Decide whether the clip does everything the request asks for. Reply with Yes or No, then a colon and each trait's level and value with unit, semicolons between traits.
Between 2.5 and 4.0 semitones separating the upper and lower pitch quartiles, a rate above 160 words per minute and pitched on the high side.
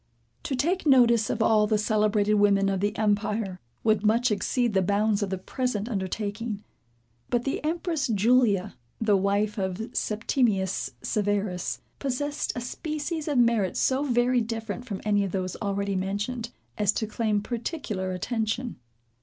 No: average, 3.2 semitones; average, 150 wpm; high, 215 Hz